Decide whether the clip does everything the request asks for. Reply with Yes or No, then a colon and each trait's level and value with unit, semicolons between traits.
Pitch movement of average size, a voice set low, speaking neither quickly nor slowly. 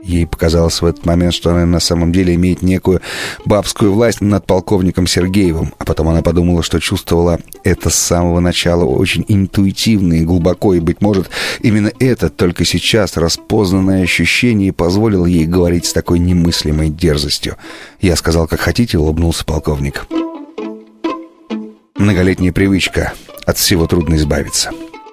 Yes: average, 3.3 semitones; very low, 90 Hz; average, 140 wpm